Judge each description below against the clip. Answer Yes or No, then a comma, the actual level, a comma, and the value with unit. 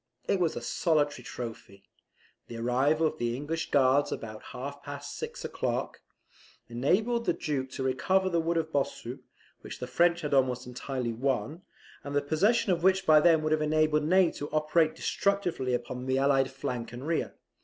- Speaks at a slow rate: No, average, 175 wpm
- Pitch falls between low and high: Yes, medium, 145 Hz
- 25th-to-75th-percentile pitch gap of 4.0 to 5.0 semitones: Yes, average, 4.3 semitones